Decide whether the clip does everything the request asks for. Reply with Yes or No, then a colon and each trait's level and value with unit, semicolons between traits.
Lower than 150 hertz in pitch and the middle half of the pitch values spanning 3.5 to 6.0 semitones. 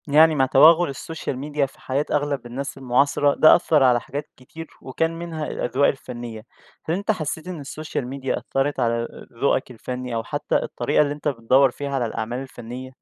No: medium, 140 Hz; average, 3.1 semitones